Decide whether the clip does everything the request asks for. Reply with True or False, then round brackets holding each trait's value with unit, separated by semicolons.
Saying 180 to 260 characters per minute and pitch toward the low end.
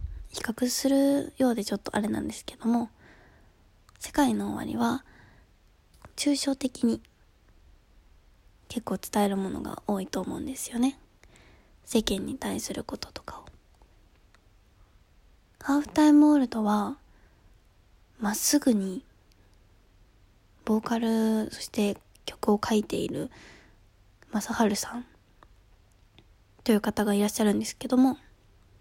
False (235 characters per minute; 205 Hz)